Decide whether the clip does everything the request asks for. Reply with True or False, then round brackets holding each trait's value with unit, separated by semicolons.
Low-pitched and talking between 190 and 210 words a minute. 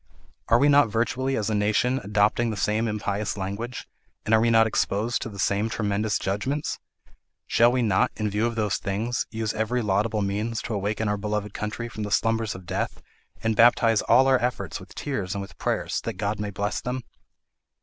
True (110 Hz; 200 wpm)